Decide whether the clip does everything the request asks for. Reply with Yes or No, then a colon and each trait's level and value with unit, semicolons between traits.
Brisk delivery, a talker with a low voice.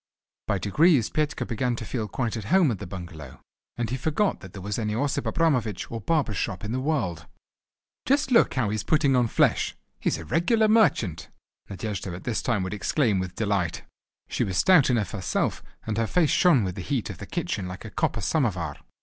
Yes: fast, 210 wpm; low, 115 Hz